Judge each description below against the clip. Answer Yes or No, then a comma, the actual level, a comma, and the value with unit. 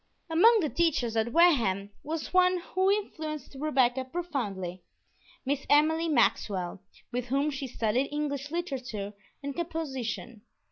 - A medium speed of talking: No, slow, 125 wpm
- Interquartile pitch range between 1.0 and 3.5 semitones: No, wide, 5.5 semitones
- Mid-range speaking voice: No, very high, 280 Hz